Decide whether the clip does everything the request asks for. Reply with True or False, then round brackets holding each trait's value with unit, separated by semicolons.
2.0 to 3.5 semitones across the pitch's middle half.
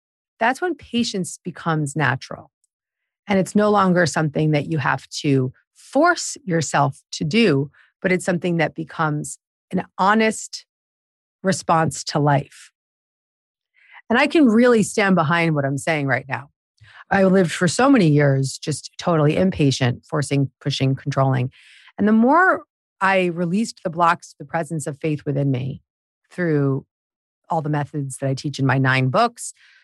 False (5.3 semitones)